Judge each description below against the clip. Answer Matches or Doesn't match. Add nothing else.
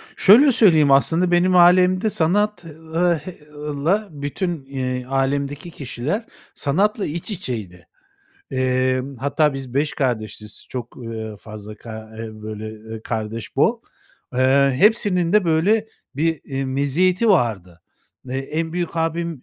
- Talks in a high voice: Doesn't match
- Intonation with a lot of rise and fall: Matches